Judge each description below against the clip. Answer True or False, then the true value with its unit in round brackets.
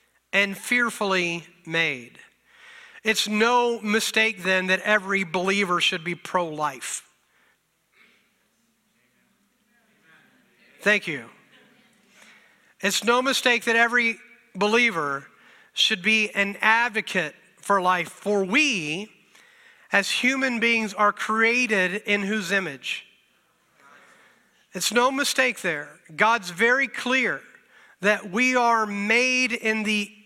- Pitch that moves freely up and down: False (3.9 semitones)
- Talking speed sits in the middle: False (100 wpm)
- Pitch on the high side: True (210 Hz)